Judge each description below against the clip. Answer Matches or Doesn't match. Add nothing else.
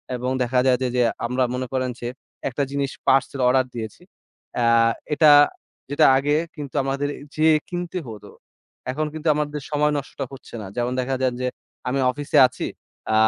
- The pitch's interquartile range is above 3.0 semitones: Doesn't match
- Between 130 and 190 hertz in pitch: Matches